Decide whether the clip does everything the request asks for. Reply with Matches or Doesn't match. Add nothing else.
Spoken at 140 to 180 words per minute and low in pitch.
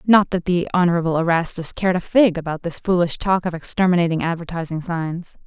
Doesn't match